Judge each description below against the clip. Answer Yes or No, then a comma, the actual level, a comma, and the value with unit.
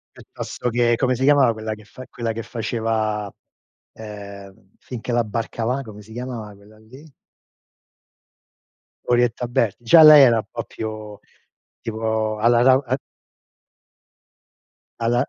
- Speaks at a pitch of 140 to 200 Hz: No, low, 115 Hz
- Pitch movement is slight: Yes, narrow, 2.1 semitones